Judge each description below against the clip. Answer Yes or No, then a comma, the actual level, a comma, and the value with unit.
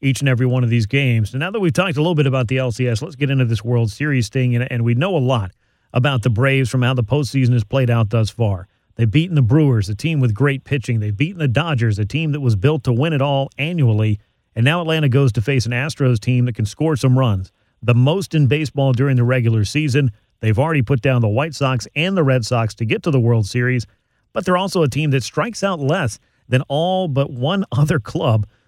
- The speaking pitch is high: No, low, 130 Hz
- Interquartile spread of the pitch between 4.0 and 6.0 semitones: No, average, 3.6 semitones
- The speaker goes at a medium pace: No, fast, 250 wpm